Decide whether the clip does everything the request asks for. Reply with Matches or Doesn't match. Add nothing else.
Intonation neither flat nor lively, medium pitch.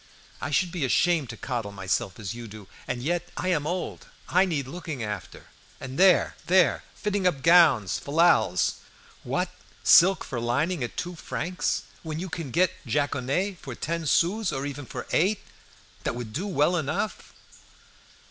Doesn't match